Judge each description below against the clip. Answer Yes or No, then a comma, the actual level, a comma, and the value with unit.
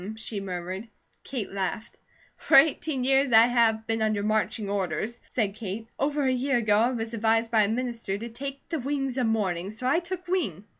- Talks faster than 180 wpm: Yes, average, 195 wpm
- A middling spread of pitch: Yes, average, 3.9 semitones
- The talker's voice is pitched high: Yes, high, 225 Hz